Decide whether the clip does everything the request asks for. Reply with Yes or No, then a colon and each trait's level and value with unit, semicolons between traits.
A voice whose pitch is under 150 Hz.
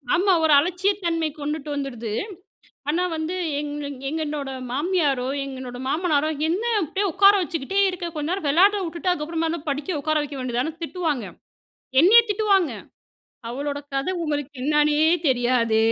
No: very high, 310 Hz